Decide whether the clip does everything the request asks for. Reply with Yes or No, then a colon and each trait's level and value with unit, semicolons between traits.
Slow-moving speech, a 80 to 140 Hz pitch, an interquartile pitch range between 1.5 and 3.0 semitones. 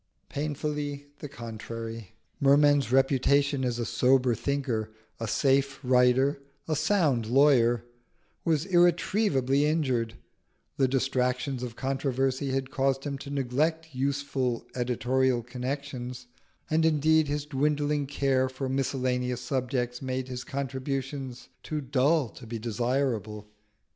Yes: slow, 115 wpm; low, 135 Hz; narrow, 2.4 semitones